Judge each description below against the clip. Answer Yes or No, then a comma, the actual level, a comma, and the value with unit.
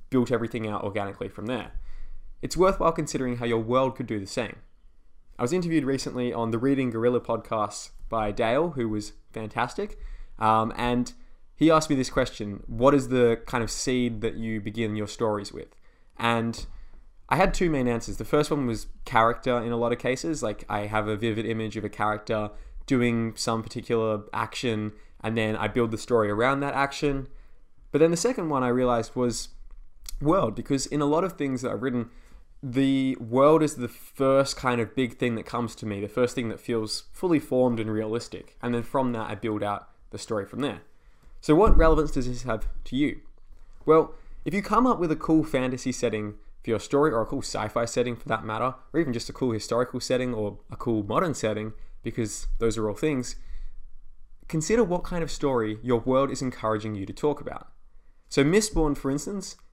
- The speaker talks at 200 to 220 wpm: Yes, fast, 205 wpm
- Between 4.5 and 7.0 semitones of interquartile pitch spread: No, average, 3.9 semitones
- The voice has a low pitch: Yes, low, 120 Hz